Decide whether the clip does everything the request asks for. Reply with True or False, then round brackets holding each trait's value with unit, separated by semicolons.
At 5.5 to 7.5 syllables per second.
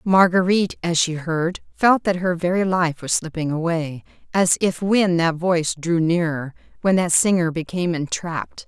False (4.8 syllables/s)